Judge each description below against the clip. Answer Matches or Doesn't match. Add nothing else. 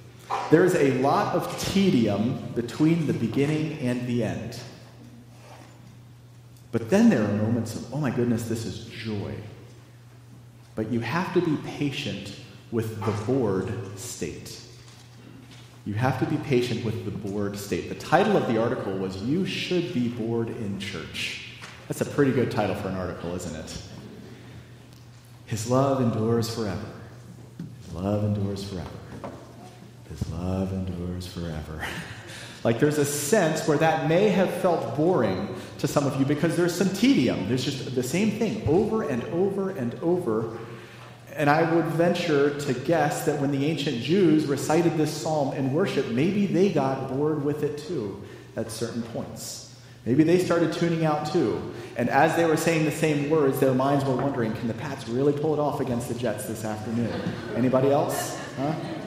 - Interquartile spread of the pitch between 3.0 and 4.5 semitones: Doesn't match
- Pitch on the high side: Doesn't match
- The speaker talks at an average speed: Matches